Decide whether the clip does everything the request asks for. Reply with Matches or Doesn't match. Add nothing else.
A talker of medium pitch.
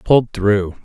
Doesn't match